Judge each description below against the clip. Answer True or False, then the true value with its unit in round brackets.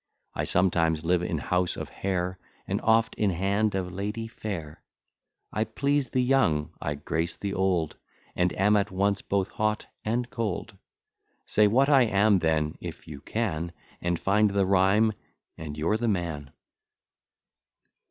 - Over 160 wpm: False (150 wpm)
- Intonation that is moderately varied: True (4.0 semitones)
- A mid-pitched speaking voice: False (95 Hz)